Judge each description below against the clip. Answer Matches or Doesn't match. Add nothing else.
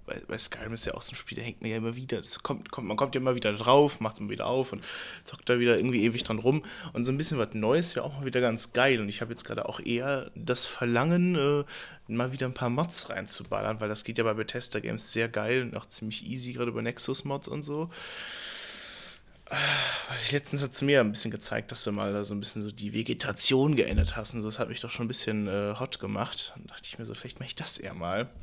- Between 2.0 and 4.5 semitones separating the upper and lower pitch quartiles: Matches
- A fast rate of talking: Matches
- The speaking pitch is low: Matches